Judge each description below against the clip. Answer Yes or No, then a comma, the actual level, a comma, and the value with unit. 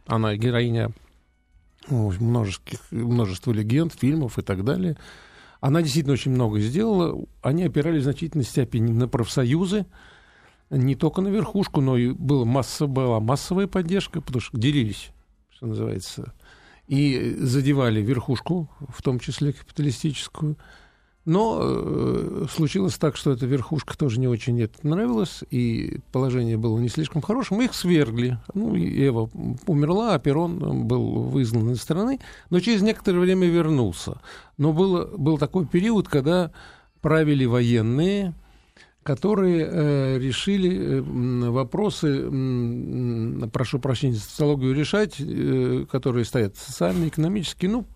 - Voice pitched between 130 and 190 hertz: Yes, medium, 140 Hz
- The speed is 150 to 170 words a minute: No, average, 130 wpm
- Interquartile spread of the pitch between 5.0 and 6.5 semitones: Yes, wide, 5.5 semitones